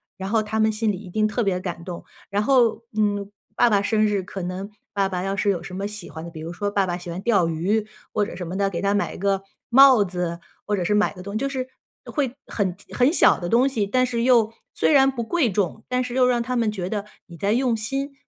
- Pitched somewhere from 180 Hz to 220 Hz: Yes, high, 205 Hz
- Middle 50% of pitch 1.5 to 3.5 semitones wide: No, average, 3.9 semitones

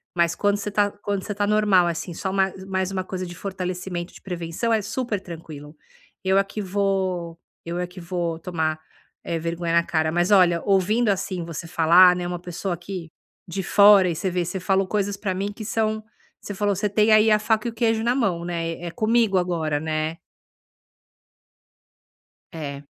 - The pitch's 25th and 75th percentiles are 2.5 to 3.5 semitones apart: Yes, average, 3.1 semitones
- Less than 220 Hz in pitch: Yes, medium, 185 Hz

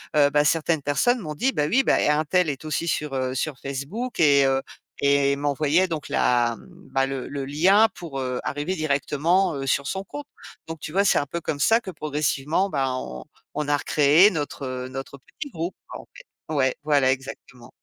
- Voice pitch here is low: No, medium, 145 Hz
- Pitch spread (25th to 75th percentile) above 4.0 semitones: No, average, 3.7 semitones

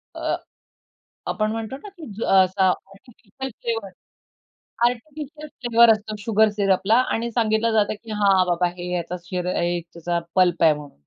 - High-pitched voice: Yes, high, 215 Hz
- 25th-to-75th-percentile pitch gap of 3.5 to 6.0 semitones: Yes, average, 4.0 semitones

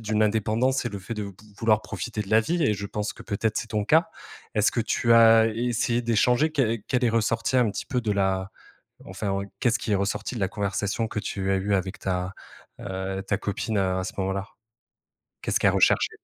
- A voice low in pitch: Yes, low, 110 Hz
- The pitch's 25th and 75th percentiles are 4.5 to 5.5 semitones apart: No, average, 2.9 semitones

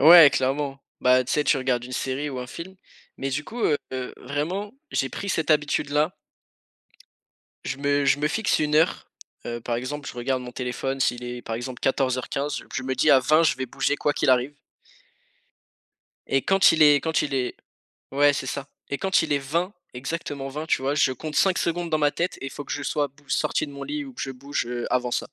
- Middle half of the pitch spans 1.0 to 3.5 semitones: Yes, average, 2.8 semitones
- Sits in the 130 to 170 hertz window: Yes, medium, 140 Hz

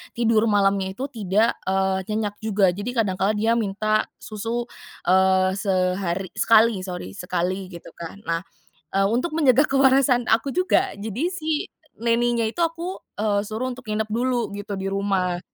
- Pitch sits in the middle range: No, high, 215 Hz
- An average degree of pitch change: Yes, average, 3.7 semitones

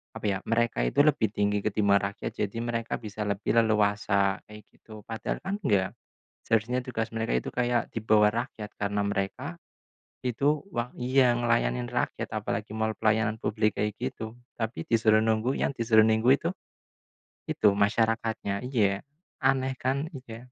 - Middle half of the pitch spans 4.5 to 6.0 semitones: No, average, 2.7 semitones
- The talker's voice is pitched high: No, low, 110 Hz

